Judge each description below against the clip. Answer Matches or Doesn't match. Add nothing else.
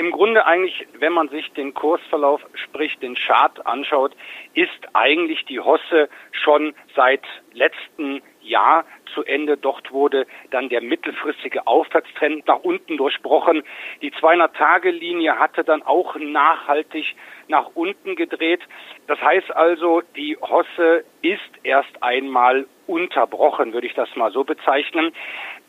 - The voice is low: Doesn't match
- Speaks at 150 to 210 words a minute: Doesn't match